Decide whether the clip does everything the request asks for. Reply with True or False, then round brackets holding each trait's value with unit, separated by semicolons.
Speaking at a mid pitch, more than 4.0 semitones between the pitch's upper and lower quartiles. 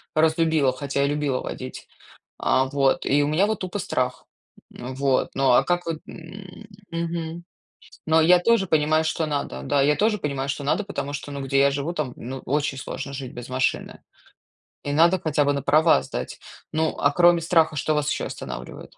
False (150 Hz; 3.4 semitones)